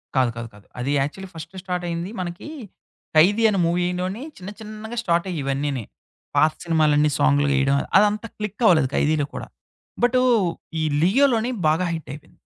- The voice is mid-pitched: Yes, medium, 170 Hz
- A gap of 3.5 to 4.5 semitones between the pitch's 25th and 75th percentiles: No, wide, 5.5 semitones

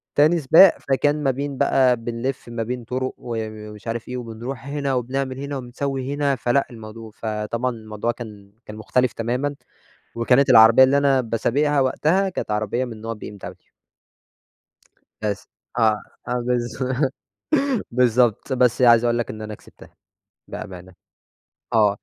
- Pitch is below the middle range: Yes, low, 120 Hz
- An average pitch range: Yes, average, 3.1 semitones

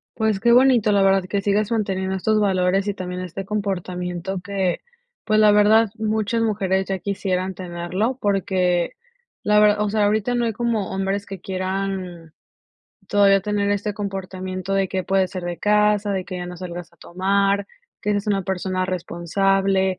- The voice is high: Yes, high, 195 Hz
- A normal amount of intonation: No, narrow, 2.0 semitones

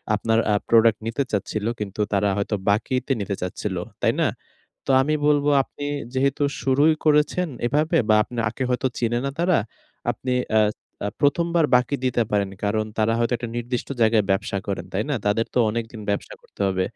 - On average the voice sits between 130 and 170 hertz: No, low, 115 Hz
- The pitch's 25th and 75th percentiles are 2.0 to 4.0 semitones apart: No, average, 4.8 semitones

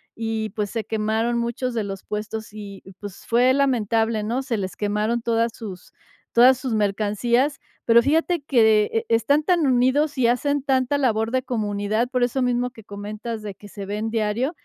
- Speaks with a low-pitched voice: No, high, 230 Hz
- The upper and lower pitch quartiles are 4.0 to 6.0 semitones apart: No, average, 3.2 semitones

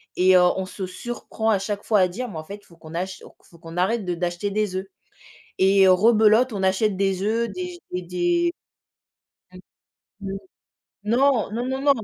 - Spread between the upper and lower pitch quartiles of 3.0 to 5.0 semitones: Yes, average, 3.9 semitones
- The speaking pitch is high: Yes, high, 200 Hz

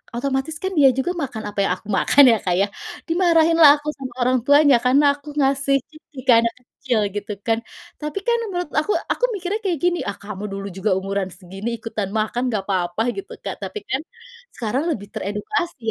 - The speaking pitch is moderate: No, very high, 265 Hz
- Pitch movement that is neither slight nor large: No, wide, 7.1 semitones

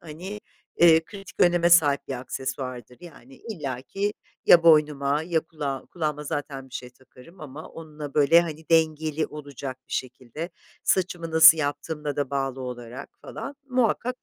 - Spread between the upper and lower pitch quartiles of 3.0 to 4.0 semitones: Yes, average, 3.6 semitones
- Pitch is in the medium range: Yes, medium, 150 Hz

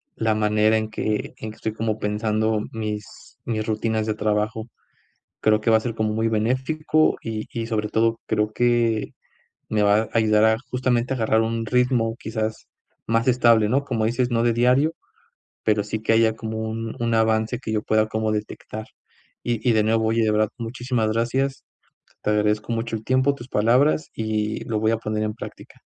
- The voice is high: No, low, 110 Hz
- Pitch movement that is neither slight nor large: No, narrow, 1.4 semitones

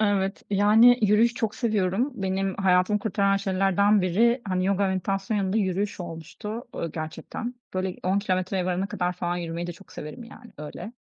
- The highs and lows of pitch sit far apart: No, narrow, 2.5 semitones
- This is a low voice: No, high, 195 Hz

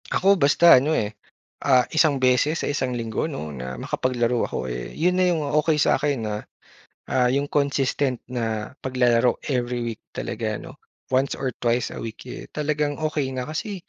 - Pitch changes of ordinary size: Yes, average, 3.8 semitones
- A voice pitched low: Yes, low, 130 Hz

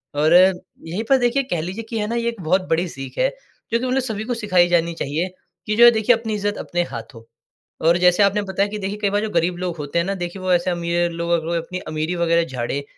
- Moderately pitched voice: Yes, medium, 180 Hz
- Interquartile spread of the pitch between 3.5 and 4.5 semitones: Yes, average, 3.8 semitones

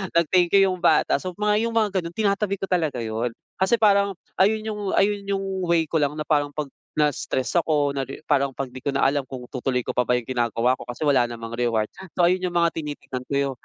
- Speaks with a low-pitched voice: No, medium, 150 Hz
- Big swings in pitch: Yes, wide, 6.5 semitones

